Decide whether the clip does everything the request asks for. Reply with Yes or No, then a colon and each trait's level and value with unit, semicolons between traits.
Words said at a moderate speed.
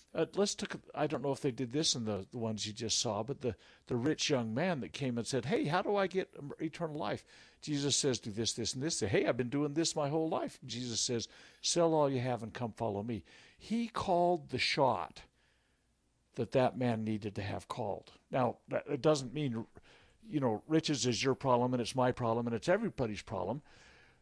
No: fast, 220 wpm